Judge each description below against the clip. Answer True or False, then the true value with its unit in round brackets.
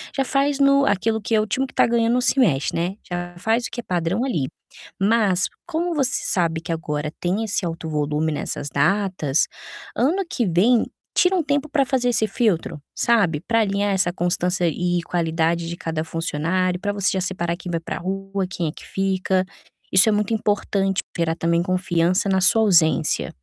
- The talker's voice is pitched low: False (190 Hz)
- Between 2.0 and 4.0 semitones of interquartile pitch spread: False (5.0 semitones)